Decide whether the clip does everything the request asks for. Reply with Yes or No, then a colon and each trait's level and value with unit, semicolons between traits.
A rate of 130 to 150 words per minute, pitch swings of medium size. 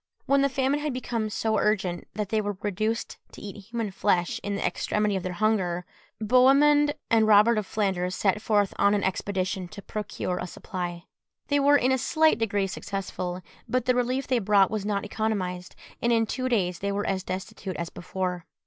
No: average, 195 wpm; average, 3.8 semitones